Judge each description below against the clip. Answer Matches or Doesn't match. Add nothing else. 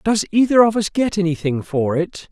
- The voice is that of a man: Matches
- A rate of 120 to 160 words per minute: Doesn't match